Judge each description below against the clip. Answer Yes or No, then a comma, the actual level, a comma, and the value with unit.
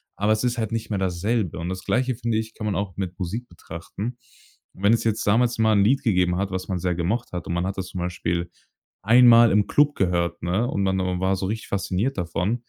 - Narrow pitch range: No, average, 4.1 semitones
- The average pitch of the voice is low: Yes, low, 100 Hz